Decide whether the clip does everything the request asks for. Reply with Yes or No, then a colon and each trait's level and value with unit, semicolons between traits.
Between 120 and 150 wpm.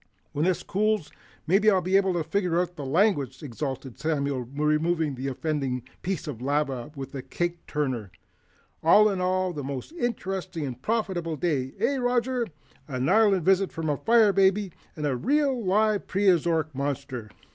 No: average, 170 wpm